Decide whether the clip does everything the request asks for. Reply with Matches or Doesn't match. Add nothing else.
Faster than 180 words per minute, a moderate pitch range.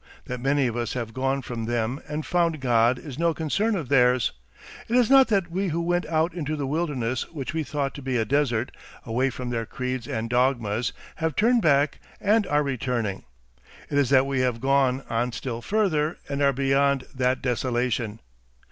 Matches